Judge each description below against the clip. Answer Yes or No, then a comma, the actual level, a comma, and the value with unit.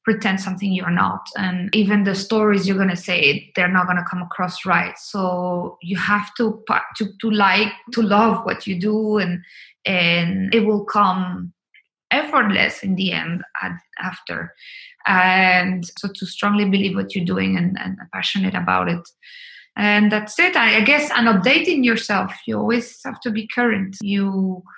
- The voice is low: No, high, 195 Hz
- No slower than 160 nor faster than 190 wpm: Yes, average, 170 wpm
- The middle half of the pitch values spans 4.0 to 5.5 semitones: No, average, 2.9 semitones